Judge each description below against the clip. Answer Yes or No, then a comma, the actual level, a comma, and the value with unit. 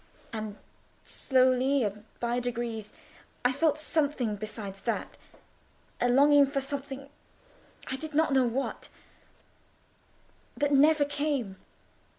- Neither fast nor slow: No, slow, 100 wpm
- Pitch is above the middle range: Yes, very high, 265 Hz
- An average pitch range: Yes, average, 3.6 semitones